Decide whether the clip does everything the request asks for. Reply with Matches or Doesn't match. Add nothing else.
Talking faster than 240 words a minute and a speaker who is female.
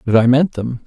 Doesn't match